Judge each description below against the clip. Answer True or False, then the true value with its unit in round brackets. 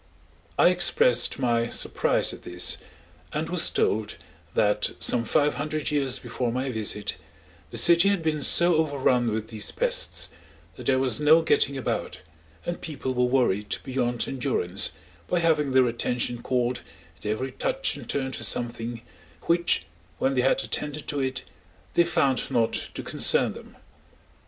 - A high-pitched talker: False (130 Hz)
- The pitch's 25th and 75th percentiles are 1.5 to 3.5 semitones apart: False (4.3 semitones)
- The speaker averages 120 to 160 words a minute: True (155 wpm)